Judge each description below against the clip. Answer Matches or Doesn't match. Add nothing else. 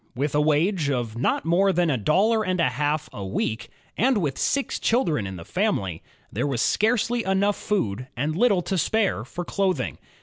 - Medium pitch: Matches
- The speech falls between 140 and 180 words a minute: Doesn't match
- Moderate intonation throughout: Doesn't match